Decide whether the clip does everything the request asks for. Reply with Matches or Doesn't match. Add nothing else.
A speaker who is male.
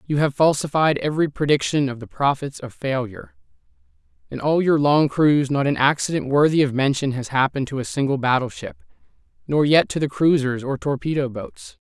Matches